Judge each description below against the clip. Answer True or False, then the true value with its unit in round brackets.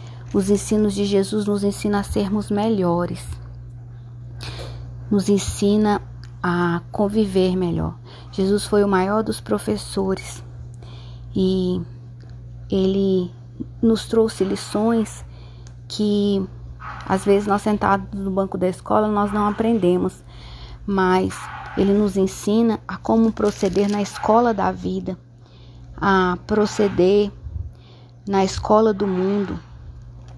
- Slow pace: True (105 wpm)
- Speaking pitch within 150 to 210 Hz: True (190 Hz)